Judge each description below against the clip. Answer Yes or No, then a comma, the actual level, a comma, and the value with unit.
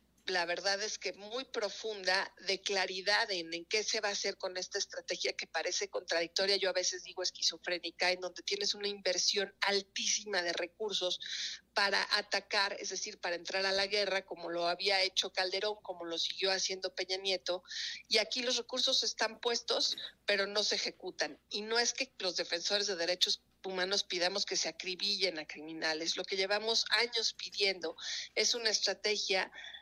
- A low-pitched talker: No, high, 195 Hz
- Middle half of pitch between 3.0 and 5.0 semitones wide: No, narrow, 2.6 semitones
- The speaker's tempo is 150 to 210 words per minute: Yes, average, 175 wpm